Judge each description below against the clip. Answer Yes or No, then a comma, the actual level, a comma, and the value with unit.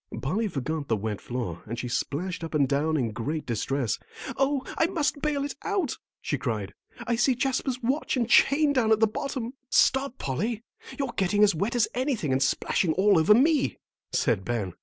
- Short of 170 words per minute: No, average, 190 wpm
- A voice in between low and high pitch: No, high, 205 Hz